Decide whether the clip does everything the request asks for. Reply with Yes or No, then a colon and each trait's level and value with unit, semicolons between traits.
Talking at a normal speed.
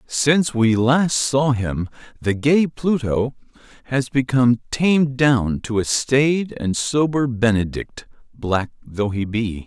No: slow, 130 wpm